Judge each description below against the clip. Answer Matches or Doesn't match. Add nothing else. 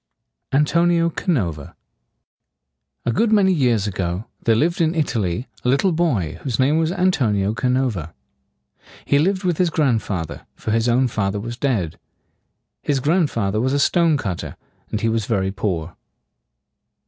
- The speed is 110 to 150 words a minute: Doesn't match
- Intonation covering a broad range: Matches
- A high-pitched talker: Doesn't match